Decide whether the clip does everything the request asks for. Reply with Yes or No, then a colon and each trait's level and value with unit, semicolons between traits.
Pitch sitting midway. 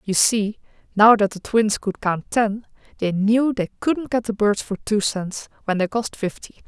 No: high, 215 Hz